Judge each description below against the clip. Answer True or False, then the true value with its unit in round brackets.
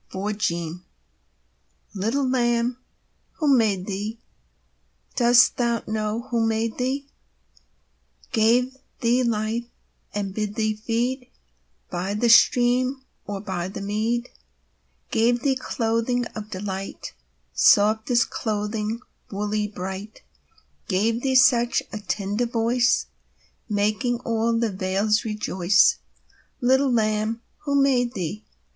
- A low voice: False (225 Hz)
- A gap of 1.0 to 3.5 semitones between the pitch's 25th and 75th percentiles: True (2.7 semitones)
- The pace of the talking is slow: True (110 wpm)